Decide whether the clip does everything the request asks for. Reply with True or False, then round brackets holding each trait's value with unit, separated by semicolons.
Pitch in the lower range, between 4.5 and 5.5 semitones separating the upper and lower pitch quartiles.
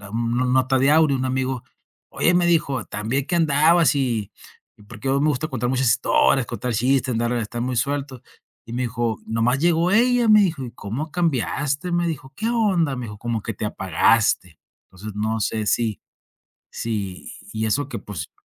True (130 Hz; 4.9 semitones)